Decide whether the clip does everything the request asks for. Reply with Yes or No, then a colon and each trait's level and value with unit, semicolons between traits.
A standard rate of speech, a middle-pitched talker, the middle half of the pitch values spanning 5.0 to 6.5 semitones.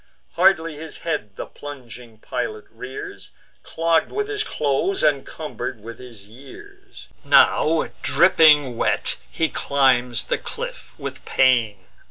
No: slow, 125 wpm; medium, 145 Hz; wide, 5.5 semitones